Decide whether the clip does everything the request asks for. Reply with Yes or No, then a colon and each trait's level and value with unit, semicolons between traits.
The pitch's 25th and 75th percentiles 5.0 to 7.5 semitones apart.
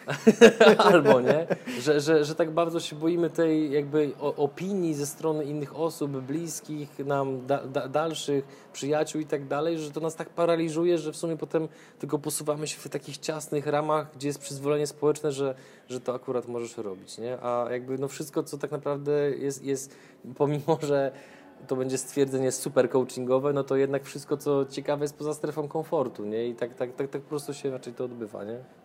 No: narrow, 2.4 semitones